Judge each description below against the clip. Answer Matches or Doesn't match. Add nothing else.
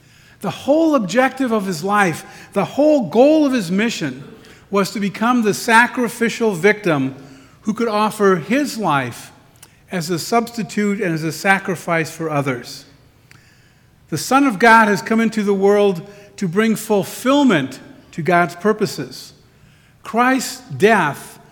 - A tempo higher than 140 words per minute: Doesn't match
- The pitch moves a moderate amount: Doesn't match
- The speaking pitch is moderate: Doesn't match